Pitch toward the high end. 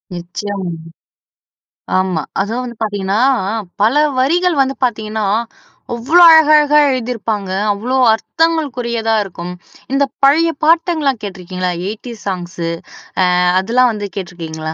Yes: high, 225 Hz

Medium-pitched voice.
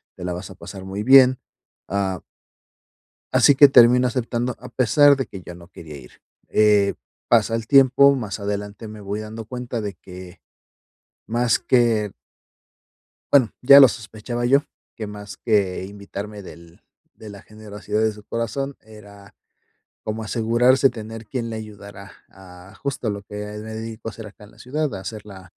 No: low, 110 Hz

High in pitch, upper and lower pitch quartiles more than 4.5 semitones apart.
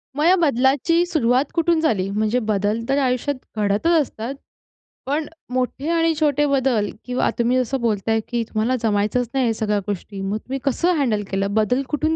Yes: very high, 250 Hz; average, 5.1 semitones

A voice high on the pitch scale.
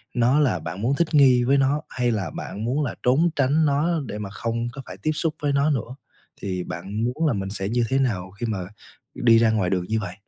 No: low, 120 Hz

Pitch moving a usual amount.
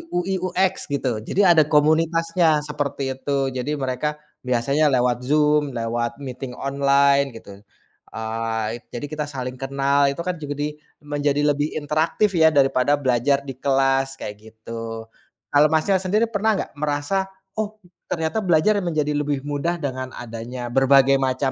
Yes: average, 3.2 semitones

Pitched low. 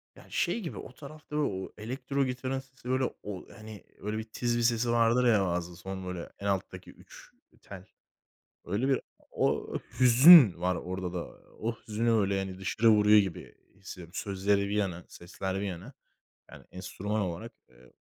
Yes: low, 105 Hz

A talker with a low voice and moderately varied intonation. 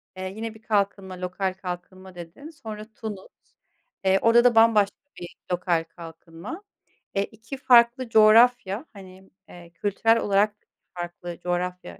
No: high, 195 Hz; average, 3.8 semitones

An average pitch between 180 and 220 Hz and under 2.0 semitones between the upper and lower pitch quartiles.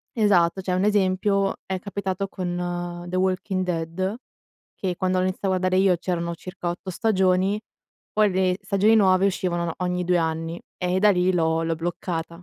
Yes: medium, 185 Hz; narrow, 1.6 semitones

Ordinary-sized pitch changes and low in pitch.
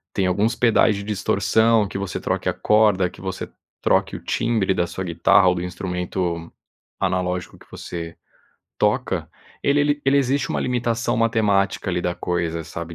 Yes: average, 4.2 semitones; very low, 95 Hz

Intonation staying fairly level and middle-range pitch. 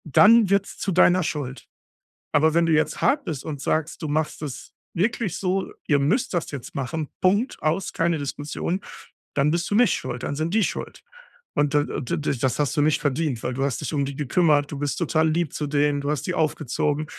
No: average, 3.2 semitones; medium, 155 Hz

